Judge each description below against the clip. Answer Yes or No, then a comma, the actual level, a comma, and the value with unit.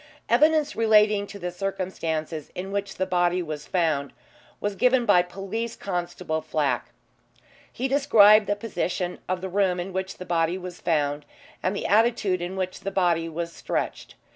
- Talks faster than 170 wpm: No, average, 165 wpm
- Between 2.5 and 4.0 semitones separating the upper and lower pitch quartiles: Yes, average, 2.8 semitones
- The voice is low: No, medium, 185 Hz